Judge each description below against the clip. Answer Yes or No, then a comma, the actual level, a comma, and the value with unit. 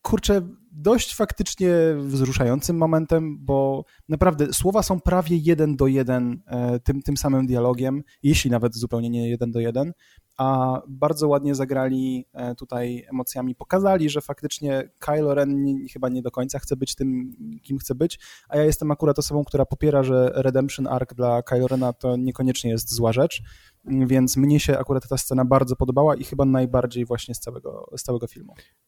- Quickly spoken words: Yes, fast, 170 wpm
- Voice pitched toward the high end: No, low, 135 Hz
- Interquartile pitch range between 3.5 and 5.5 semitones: No, average, 2.9 semitones